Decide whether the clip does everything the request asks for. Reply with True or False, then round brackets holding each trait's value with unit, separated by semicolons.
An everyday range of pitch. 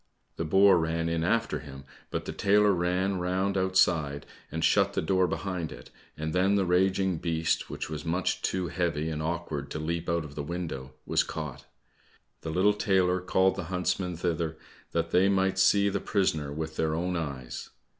True (3.1 semitones)